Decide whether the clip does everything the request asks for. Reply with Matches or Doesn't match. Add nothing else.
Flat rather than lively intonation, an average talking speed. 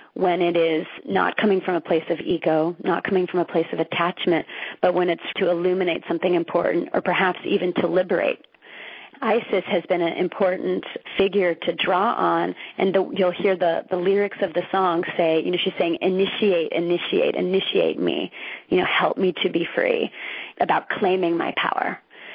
Matches